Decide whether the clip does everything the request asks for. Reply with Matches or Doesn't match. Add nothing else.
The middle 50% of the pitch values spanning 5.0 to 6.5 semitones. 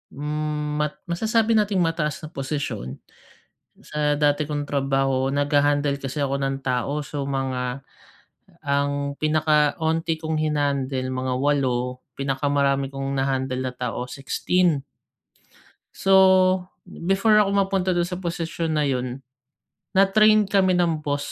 Doesn't match